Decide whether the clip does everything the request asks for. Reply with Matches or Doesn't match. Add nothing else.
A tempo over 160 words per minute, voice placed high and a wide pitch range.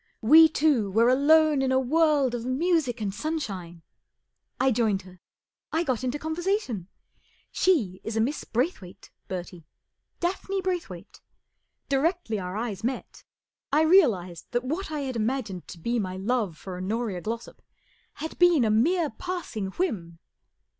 Doesn't match